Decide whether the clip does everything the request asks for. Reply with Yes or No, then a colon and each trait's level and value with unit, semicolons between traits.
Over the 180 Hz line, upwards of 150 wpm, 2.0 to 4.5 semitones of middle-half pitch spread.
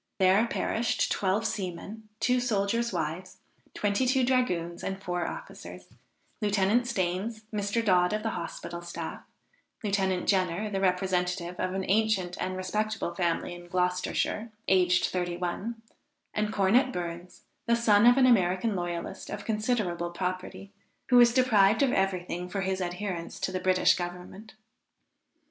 No: high, 190 Hz; average, 145 wpm; average, 3.5 semitones